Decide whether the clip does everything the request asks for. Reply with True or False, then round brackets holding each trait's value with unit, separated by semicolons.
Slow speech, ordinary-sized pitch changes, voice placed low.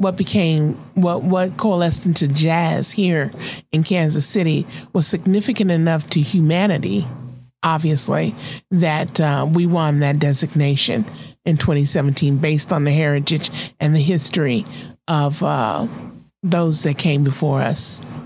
False (130 wpm; 3.2 semitones; 160 Hz)